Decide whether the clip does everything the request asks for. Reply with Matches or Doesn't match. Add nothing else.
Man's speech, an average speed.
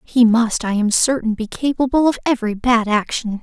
Doesn't match